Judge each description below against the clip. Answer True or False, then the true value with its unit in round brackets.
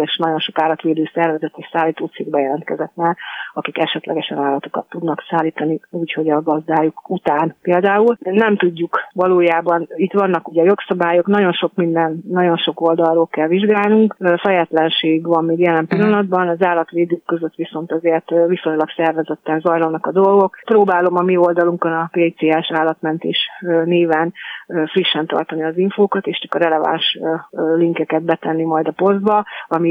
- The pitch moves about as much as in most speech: False (2.1 semitones)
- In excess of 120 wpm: True (140 wpm)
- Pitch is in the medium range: True (165 Hz)